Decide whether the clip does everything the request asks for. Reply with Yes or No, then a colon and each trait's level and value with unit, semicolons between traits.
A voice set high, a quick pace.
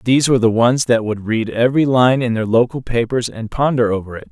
No: low, 120 Hz; fast, 235 wpm